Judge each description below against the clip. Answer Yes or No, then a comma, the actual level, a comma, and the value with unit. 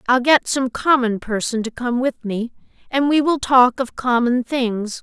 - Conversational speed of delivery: Yes, average, 190 wpm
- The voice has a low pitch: No, high, 245 Hz